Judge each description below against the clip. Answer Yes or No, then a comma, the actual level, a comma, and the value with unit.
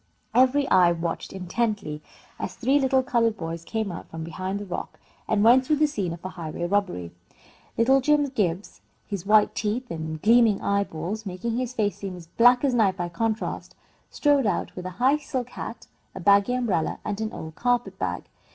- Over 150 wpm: Yes, average, 190 wpm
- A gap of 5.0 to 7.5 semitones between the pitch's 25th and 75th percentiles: Yes, wide, 5.6 semitones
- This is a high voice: Yes, high, 210 Hz